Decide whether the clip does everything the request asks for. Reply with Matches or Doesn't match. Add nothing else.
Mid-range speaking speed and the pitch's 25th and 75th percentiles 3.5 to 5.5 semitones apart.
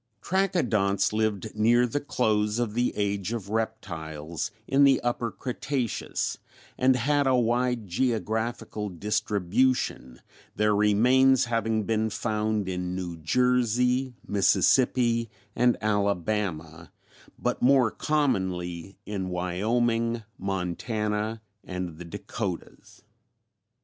Doesn't match